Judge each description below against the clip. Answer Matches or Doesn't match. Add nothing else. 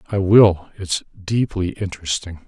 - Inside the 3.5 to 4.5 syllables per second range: Matches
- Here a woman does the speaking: Doesn't match